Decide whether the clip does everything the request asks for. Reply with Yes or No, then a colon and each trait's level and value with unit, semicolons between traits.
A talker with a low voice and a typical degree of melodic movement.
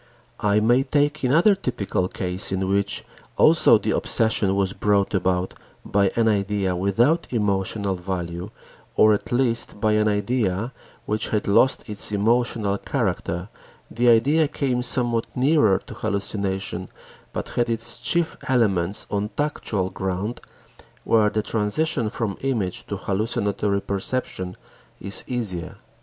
Yes: low, 105 Hz; average, 3.7 semitones